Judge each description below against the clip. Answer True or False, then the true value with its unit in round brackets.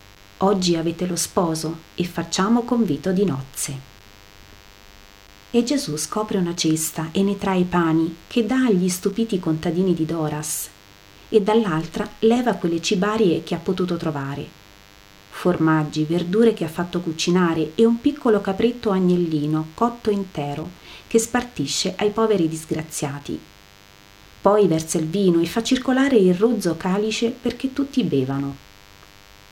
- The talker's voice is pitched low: False (170 Hz)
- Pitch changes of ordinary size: False (6.2 semitones)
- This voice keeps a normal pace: True (135 wpm)